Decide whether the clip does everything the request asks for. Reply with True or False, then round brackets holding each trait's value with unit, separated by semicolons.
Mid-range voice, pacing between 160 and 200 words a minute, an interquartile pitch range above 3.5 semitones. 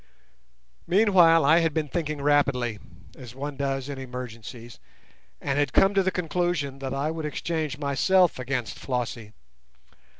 False (145 Hz; 140 wpm; 4.2 semitones)